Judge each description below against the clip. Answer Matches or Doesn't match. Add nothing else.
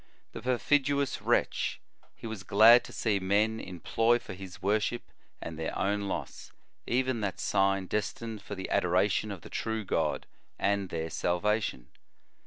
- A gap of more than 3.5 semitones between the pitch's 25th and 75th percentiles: Doesn't match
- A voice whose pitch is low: Matches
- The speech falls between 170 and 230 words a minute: Doesn't match